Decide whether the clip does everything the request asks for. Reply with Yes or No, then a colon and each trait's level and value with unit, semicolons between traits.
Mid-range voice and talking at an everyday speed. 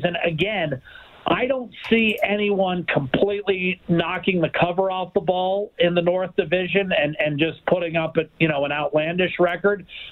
Yes: medium, 180 Hz; average, 165 wpm